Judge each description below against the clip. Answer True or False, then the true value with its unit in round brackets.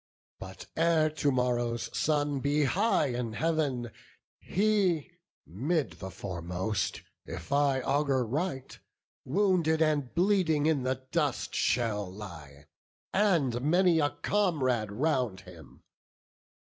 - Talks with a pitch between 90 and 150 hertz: True (140 Hz)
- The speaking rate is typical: False (110 wpm)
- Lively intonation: True (5.7 semitones)